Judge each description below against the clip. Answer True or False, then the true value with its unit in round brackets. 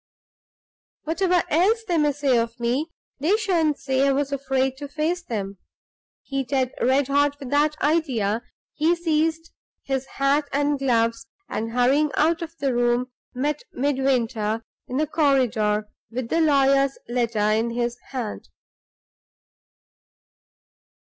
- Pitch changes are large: False (3.9 semitones)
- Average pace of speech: False (130 wpm)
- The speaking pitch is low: False (275 Hz)